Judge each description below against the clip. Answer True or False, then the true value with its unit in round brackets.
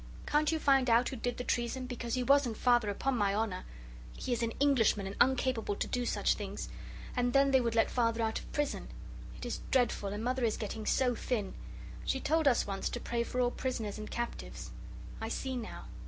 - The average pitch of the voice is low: False (240 Hz)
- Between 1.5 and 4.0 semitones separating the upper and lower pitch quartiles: True (2.7 semitones)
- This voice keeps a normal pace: False (215 wpm)